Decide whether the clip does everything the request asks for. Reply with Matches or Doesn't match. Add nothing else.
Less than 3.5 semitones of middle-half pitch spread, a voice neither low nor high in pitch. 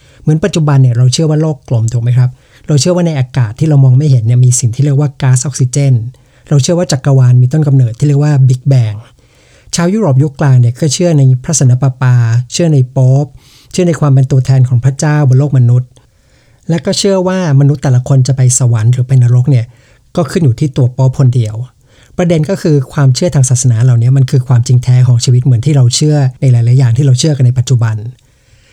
Doesn't match